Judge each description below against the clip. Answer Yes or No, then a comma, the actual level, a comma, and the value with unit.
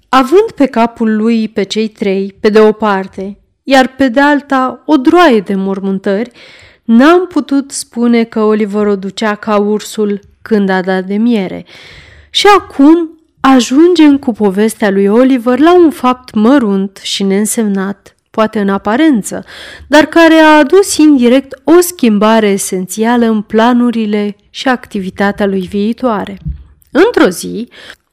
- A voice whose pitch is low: No, high, 225 Hz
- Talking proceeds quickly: No, average, 140 wpm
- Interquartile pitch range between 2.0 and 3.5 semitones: No, average, 5.2 semitones